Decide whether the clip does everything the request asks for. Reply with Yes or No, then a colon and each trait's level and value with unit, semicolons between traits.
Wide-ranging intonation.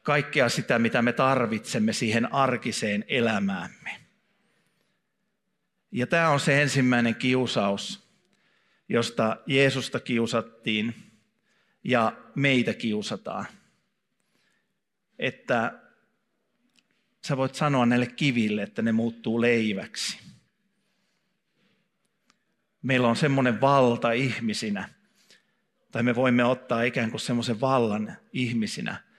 Yes: wide, 8.9 semitones